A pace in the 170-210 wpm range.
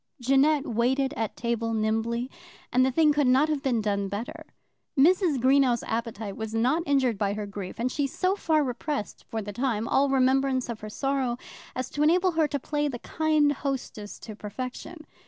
Yes: average, 185 wpm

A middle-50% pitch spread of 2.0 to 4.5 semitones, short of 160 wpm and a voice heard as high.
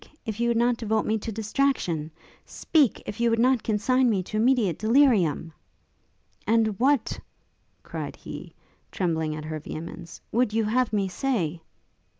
No: average, 4.9 semitones; average, 150 wpm; high, 220 Hz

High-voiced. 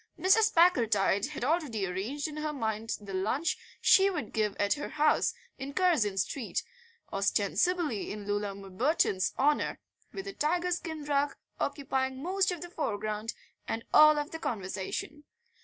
Yes: very high, 280 Hz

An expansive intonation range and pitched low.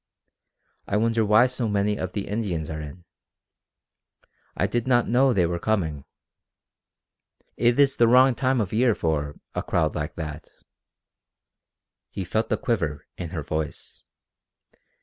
Yes: wide, 6.5 semitones; low, 105 Hz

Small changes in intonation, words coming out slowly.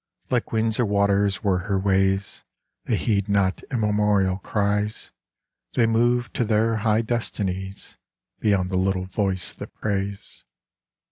Yes: narrow, 2.2 semitones; slow, 130 wpm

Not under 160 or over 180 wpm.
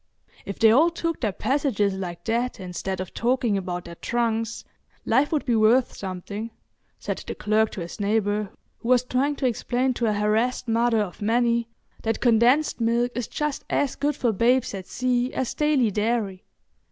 Yes: average, 175 wpm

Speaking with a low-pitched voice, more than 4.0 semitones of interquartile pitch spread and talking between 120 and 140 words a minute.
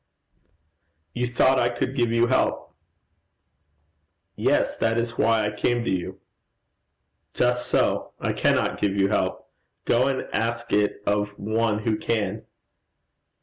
No: low, 115 Hz; narrow, 2.5 semitones; slow, 135 wpm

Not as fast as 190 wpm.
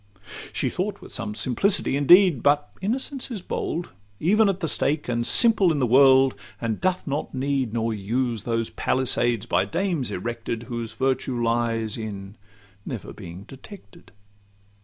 Yes: average, 150 wpm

